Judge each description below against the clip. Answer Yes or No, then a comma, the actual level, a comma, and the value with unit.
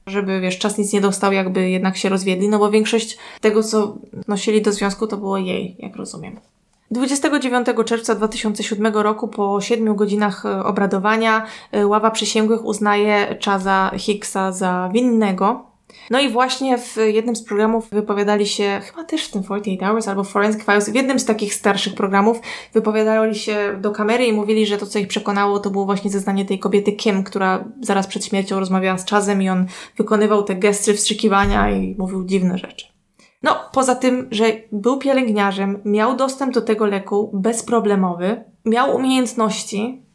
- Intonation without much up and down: Yes, narrow, 1.9 semitones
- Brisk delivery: Yes, fast, 165 wpm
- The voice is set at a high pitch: Yes, high, 210 Hz